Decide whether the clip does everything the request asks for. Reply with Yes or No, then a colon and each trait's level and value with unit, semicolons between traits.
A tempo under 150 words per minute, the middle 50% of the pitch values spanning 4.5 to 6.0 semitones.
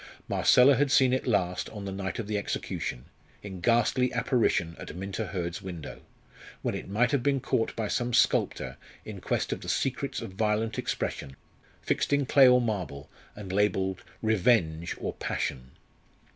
No: average, 165 wpm; average, 5.0 semitones